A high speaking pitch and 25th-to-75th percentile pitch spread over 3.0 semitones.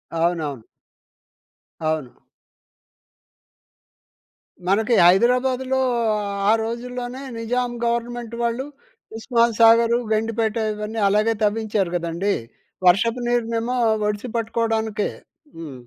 No: high, 225 Hz; narrow, 2.6 semitones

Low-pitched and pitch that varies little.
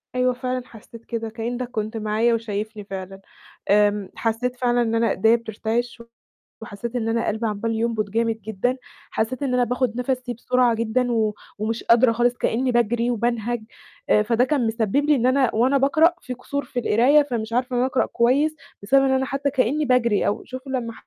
No: high, 235 Hz; narrow, 2.3 semitones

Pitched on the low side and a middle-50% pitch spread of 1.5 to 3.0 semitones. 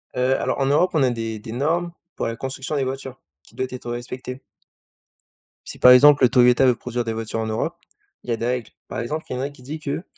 Yes: low, 125 Hz; narrow, 2.5 semitones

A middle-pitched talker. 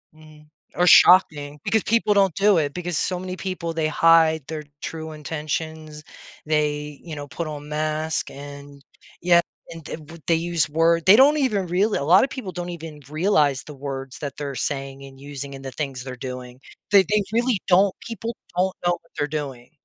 Yes: medium, 155 Hz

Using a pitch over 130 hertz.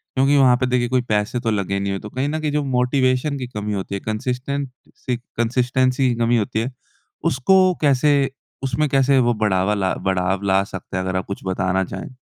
No: low, 125 Hz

